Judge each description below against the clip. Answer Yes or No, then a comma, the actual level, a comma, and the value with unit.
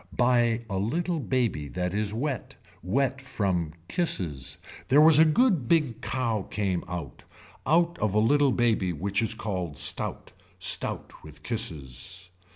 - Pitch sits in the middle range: No, low, 110 Hz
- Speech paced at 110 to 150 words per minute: Yes, average, 145 wpm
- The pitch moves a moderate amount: No, wide, 6.8 semitones